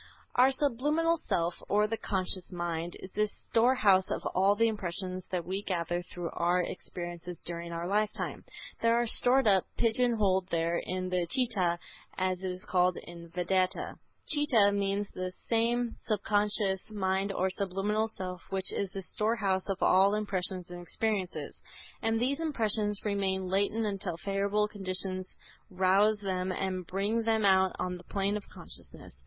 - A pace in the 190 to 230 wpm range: No, average, 155 wpm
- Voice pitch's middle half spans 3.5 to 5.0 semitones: No, average, 2.7 semitones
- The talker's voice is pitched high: Yes, high, 195 Hz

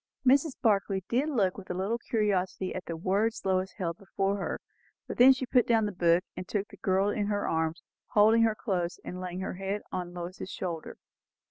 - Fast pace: Yes, fast, 210 wpm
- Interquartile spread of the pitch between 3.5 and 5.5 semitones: No, average, 2.9 semitones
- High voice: Yes, high, 195 Hz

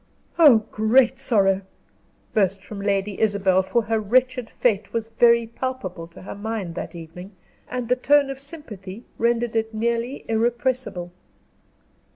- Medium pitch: No, high, 225 Hz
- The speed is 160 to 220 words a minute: No, average, 140 wpm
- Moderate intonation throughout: Yes, average, 3.7 semitones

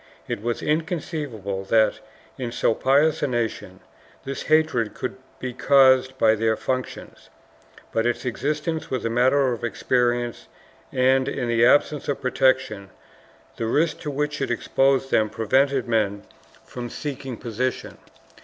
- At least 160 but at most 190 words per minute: No, average, 145 wpm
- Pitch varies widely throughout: No, average, 3.2 semitones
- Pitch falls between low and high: No, low, 130 Hz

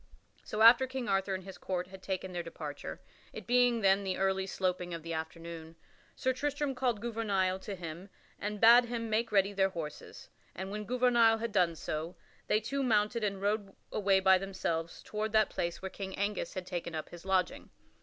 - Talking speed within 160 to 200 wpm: Yes, average, 195 wpm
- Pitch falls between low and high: No, high, 195 Hz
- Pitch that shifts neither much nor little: Yes, average, 3.6 semitones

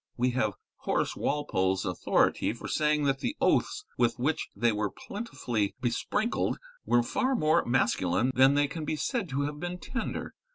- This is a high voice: No, low, 135 Hz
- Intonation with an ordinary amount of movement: Yes, average, 5.0 semitones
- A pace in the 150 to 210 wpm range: Yes, average, 165 wpm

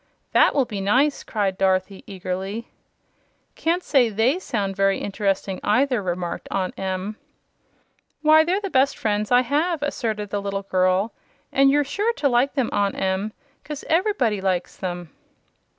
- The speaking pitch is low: No, high, 210 Hz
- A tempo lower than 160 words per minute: Yes, average, 150 wpm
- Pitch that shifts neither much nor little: No, wide, 6.3 semitones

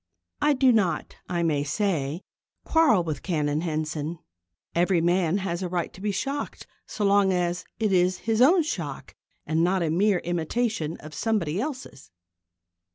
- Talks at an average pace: Yes, average, 160 wpm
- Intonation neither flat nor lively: Yes, average, 4.5 semitones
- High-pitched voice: No, medium, 180 Hz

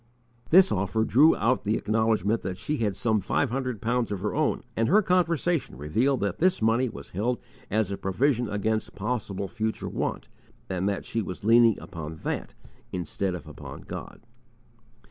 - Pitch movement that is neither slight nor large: Yes, average, 4.2 semitones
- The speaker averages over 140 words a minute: Yes, average, 170 wpm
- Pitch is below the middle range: Yes, low, 110 Hz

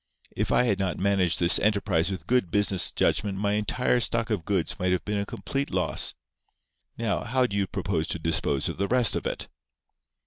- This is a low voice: Yes, low, 100 Hz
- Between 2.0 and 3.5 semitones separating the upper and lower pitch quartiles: Yes, average, 3.1 semitones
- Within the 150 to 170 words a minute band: No, average, 200 wpm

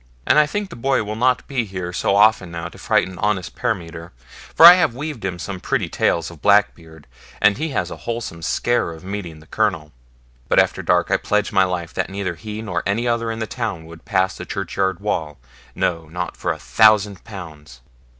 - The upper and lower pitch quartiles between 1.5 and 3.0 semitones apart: No, average, 4.7 semitones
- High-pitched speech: No, low, 100 Hz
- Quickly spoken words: Yes, fast, 210 wpm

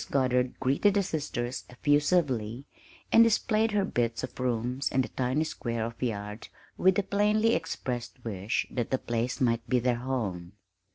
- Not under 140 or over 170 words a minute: Yes, average, 160 wpm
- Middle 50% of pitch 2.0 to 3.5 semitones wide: No, average, 5.1 semitones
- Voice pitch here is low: Yes, low, 125 Hz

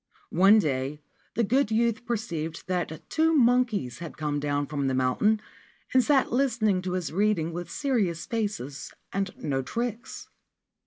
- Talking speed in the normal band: Yes, average, 150 wpm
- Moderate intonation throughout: No, wide, 7.4 semitones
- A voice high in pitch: Yes, high, 195 Hz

